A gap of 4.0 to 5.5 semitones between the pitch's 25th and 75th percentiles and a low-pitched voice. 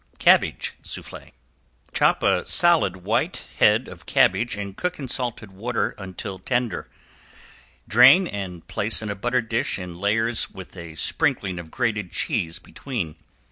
Yes: average, 4.7 semitones; low, 105 Hz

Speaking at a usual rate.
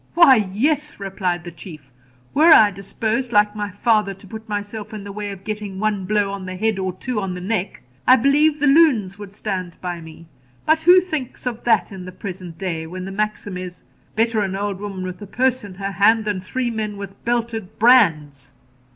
No: fast, 210 wpm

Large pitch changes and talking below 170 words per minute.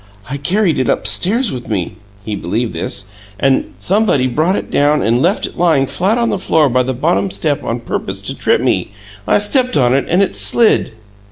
No: wide, 7.6 semitones; average, 200 wpm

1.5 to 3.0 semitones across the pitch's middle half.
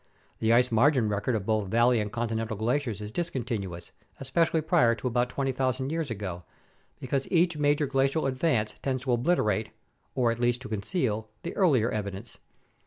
No: average, 3.9 semitones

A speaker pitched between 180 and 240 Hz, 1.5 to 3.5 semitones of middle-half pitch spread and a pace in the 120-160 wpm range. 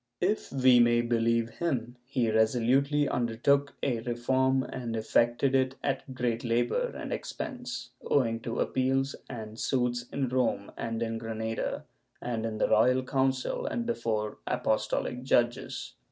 No: low, 120 Hz; narrow, 2.6 semitones; average, 140 wpm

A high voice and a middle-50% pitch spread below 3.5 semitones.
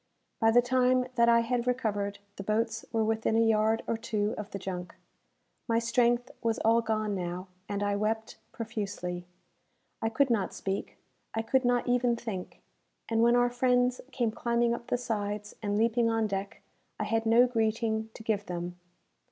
Yes: high, 225 Hz; narrow, 2.4 semitones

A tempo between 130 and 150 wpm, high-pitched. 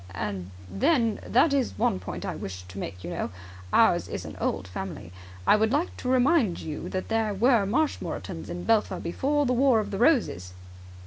No: average, 190 wpm; high, 215 Hz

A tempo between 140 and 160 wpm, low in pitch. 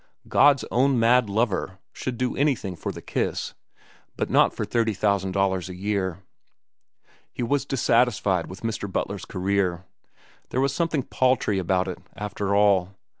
Yes: average, 150 wpm; low, 105 Hz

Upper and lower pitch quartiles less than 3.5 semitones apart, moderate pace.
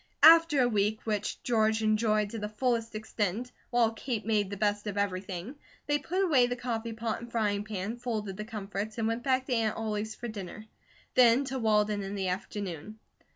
Yes: narrow, 2.6 semitones; average, 195 wpm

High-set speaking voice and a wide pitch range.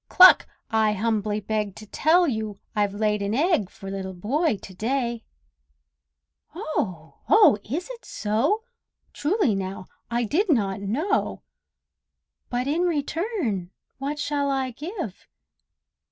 Yes: high, 235 Hz; wide, 7.2 semitones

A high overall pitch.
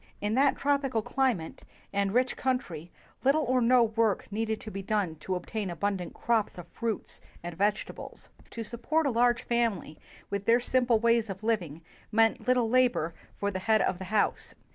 Yes: high, 220 Hz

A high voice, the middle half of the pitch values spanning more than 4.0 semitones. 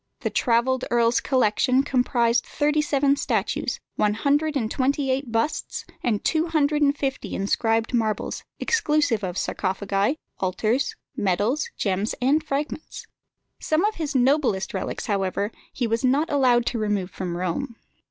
Yes: very high, 250 Hz; average, 5.1 semitones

